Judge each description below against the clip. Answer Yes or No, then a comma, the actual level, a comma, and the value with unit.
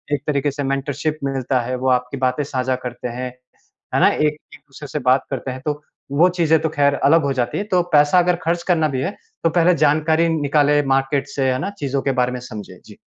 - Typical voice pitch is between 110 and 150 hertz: Yes, medium, 140 Hz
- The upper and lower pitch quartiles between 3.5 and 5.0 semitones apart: No, average, 2.8 semitones